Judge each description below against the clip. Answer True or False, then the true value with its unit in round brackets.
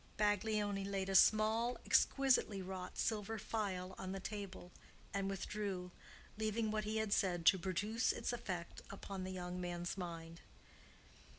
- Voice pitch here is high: True (195 Hz)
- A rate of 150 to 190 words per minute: False (140 wpm)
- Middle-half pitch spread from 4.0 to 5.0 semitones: False (2.7 semitones)